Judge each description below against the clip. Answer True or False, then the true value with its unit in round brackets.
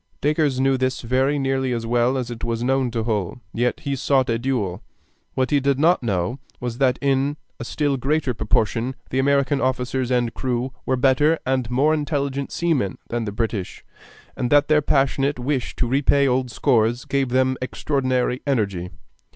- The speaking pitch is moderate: False (130 Hz)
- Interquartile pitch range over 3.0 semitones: False (2.4 semitones)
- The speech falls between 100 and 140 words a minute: False (175 wpm)